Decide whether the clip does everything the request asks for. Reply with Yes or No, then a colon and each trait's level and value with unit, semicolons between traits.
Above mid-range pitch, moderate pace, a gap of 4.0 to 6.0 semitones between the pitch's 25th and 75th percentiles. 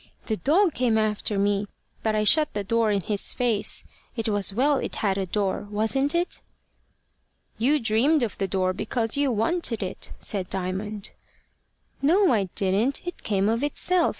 Yes: high, 220 Hz; average, 170 wpm; average, 5.2 semitones